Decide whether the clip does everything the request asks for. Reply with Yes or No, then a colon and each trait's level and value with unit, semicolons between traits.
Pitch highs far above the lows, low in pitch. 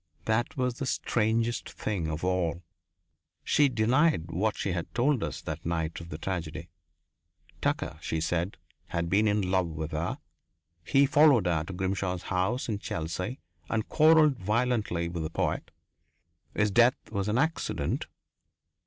Yes: wide, 6.0 semitones; low, 100 Hz